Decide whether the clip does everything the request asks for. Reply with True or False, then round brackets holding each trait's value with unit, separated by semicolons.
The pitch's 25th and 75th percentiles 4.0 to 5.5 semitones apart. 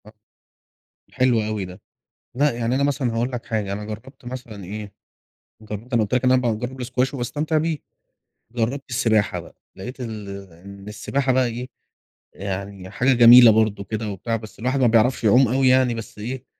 False (3.2 semitones)